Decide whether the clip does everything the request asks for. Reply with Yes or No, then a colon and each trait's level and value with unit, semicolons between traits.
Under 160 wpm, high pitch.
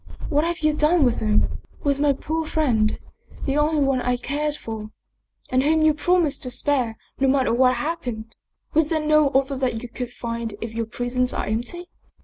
No: average, 190 wpm; very high, 270 Hz